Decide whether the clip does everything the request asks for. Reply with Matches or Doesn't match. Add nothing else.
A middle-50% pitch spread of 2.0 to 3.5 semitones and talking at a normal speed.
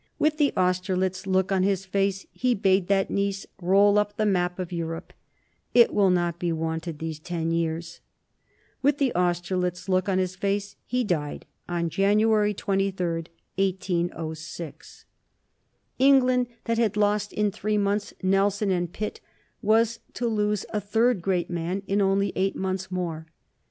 Matches